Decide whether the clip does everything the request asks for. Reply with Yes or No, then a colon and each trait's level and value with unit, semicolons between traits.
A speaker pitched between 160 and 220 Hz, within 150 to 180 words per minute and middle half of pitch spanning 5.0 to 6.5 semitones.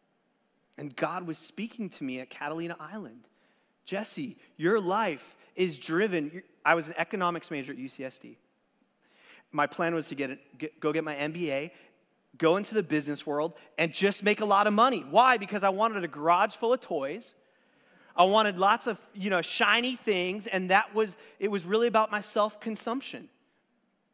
Yes: high, 190 Hz; average, 175 wpm; wide, 5.5 semitones